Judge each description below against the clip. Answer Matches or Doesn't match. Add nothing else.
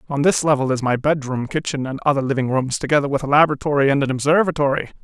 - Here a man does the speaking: Matches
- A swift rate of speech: Matches